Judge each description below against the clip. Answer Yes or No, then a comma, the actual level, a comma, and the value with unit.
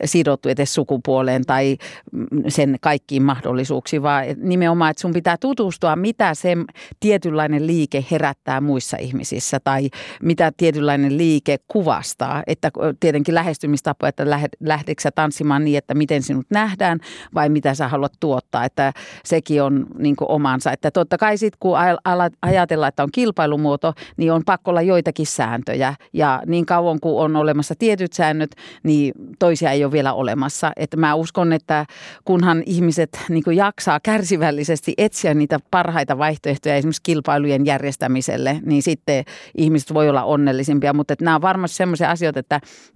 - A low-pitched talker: No, medium, 155 Hz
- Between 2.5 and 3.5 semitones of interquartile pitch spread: Yes, average, 2.9 semitones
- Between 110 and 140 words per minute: No, average, 150 wpm